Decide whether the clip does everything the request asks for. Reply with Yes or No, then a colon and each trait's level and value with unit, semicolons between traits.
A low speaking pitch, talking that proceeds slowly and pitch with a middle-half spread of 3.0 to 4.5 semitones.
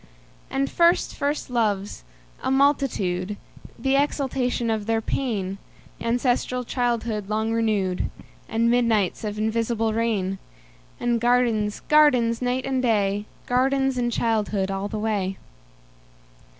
No: high, 230 Hz; slow, 100 wpm; average, 3.3 semitones